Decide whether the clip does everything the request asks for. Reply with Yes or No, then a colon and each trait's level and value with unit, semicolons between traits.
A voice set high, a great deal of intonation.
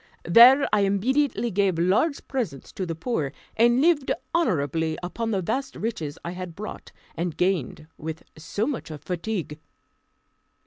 Yes: high, 195 Hz; wide, 6.6 semitones